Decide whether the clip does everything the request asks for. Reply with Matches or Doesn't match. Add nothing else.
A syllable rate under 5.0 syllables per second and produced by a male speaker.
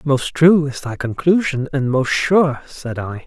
Matches